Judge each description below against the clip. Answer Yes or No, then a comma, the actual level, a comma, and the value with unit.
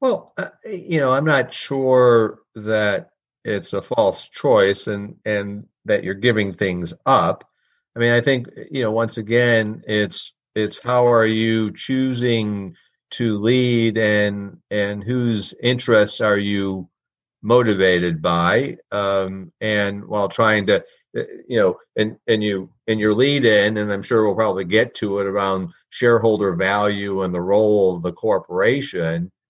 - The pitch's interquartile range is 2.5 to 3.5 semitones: Yes, average, 3.2 semitones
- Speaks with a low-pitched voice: Yes, low, 105 Hz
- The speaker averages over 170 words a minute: No, average, 150 wpm